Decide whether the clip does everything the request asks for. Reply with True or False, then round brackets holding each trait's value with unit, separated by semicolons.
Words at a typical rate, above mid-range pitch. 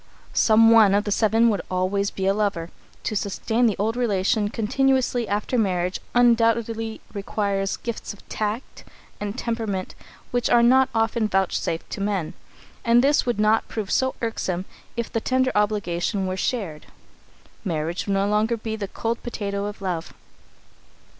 True (155 wpm; 210 Hz)